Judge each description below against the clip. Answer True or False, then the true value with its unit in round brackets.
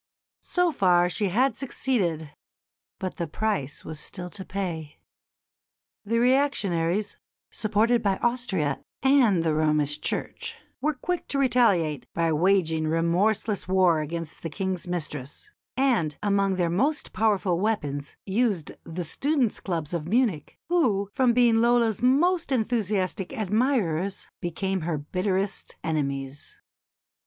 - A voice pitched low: False (190 Hz)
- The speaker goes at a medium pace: False (125 wpm)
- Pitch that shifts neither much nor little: False (6.1 semitones)